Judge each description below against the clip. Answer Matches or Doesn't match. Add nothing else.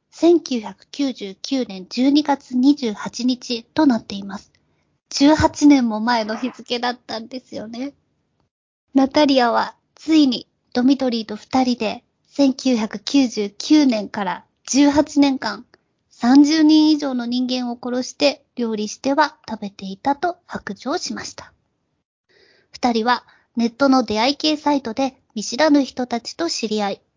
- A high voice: Matches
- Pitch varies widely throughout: Doesn't match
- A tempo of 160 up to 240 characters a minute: Matches